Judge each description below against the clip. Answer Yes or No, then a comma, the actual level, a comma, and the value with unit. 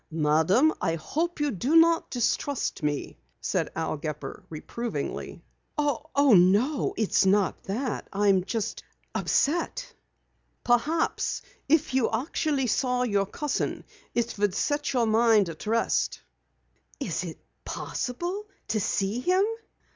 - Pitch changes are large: Yes, wide, 6.9 semitones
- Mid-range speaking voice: No, high, 240 Hz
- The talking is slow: Yes, slow, 120 wpm